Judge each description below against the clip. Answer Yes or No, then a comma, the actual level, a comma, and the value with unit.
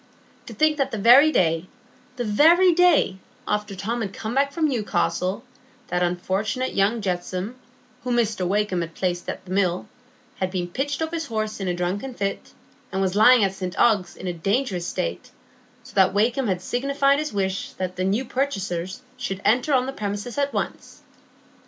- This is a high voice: Yes, high, 210 Hz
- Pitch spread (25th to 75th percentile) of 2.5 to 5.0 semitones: No, wide, 5.5 semitones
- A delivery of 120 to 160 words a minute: No, average, 175 wpm